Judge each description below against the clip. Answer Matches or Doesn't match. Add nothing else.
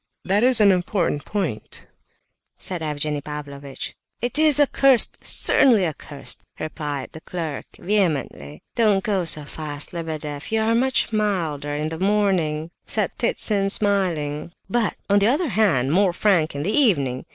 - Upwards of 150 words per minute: Doesn't match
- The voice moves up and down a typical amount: Doesn't match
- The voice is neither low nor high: Matches